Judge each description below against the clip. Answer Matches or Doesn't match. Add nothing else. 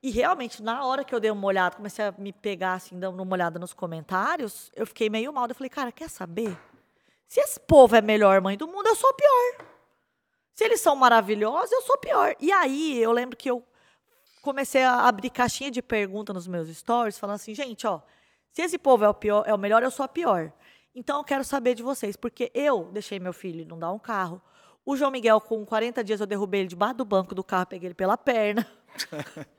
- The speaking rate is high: Matches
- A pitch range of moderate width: Matches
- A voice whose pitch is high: Matches